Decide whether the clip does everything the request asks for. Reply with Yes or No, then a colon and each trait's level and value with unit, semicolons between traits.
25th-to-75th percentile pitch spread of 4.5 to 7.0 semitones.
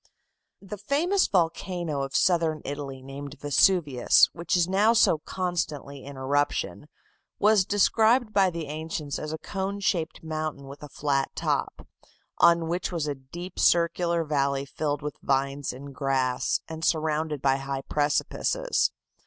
No: average, 4.1 semitones